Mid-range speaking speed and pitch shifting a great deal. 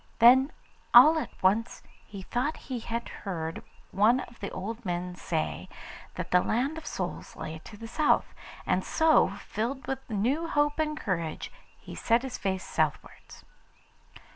Yes: average, 155 wpm; wide, 6.2 semitones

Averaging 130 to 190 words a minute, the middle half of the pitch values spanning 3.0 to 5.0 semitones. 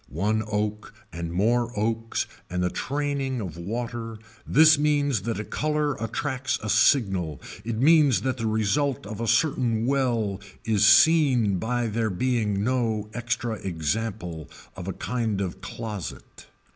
Yes: average, 145 wpm; average, 3.8 semitones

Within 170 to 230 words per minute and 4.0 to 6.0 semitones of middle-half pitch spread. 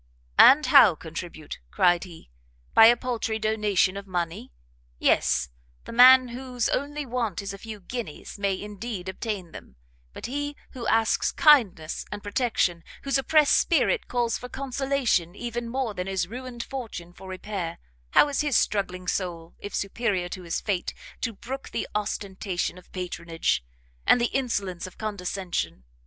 No: average, 155 wpm; average, 5.3 semitones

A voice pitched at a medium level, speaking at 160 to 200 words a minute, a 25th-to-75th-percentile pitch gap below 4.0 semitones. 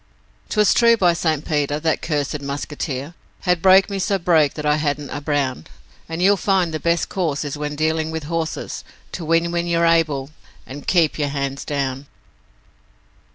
Yes: medium, 155 Hz; average, 175 wpm; average, 2.8 semitones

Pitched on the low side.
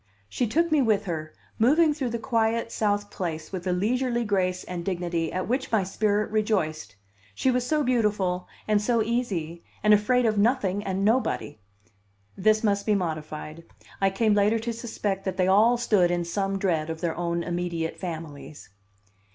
No: high, 200 Hz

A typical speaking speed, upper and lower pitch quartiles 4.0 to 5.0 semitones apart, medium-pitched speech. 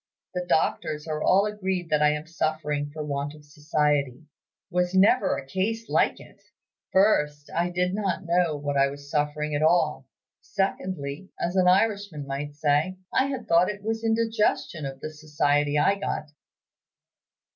Yes: average, 160 wpm; average, 4.4 semitones; medium, 155 Hz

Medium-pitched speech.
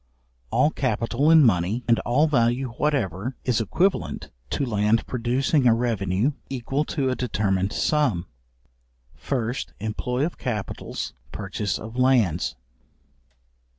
No: low, 120 Hz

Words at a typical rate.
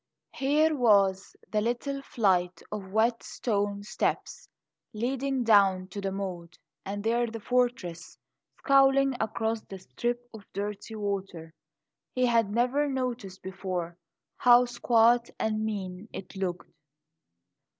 No: slow, 120 wpm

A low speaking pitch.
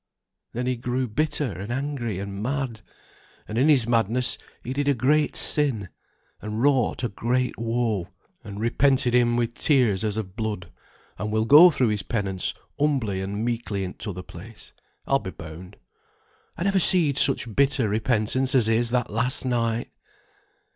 Yes: low, 120 Hz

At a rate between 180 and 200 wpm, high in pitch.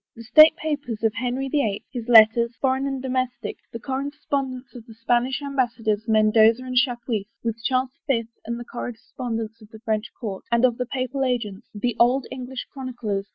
Yes: average, 190 wpm; high, 245 Hz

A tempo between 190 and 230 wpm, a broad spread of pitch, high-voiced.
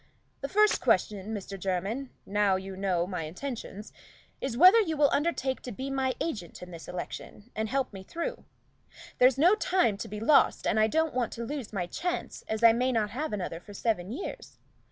Yes: average, 195 wpm; wide, 5.9 semitones; high, 225 Hz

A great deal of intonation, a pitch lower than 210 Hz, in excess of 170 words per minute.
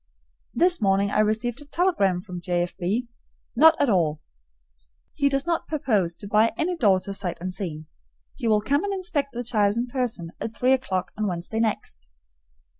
No: wide, 6.7 semitones; high, 215 Hz; average, 180 wpm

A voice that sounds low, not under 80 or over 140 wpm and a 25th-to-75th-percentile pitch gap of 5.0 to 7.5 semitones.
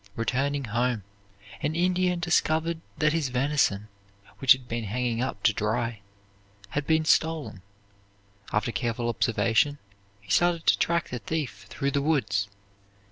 Yes: low, 130 Hz; slow, 135 wpm; wide, 5.6 semitones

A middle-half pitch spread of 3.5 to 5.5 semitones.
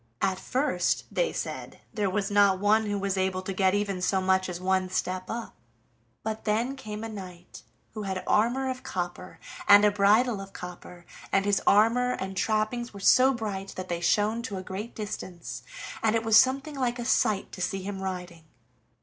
No: average, 3.0 semitones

